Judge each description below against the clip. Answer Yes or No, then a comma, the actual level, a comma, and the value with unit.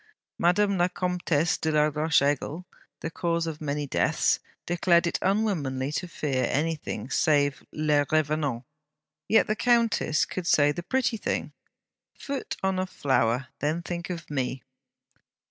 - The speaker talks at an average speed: Yes, average, 145 wpm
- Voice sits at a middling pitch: Yes, medium, 160 Hz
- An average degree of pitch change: Yes, average, 3.8 semitones